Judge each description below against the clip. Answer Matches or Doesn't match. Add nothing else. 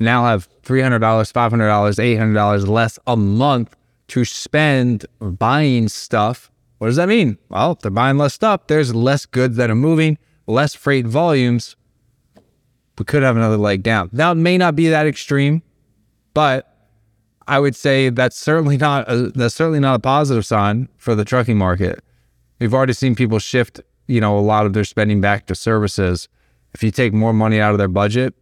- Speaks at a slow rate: Doesn't match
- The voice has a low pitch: Matches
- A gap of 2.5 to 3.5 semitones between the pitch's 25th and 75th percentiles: Doesn't match